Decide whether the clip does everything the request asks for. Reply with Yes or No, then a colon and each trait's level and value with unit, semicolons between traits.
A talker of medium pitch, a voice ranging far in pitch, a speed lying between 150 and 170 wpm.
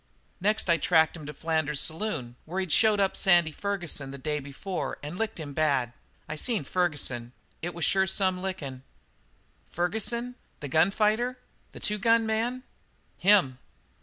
Yes: medium, 175 Hz; wide, 5.7 semitones; average, 160 wpm